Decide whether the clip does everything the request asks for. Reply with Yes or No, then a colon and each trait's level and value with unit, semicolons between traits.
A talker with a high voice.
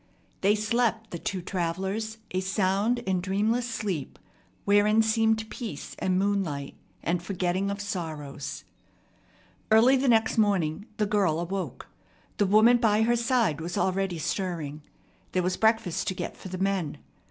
Yes: high, 195 Hz